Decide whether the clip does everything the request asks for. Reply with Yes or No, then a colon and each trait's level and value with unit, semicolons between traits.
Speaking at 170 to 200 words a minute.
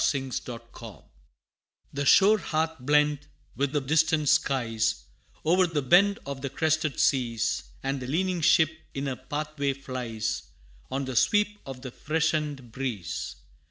No: average, 150 wpm